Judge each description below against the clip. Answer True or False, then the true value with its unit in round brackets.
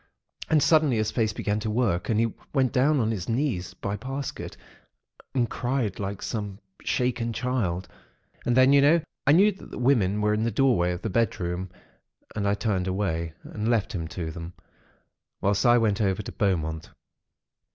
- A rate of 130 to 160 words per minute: False (185 wpm)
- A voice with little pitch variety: False (4.9 semitones)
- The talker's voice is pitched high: False (110 Hz)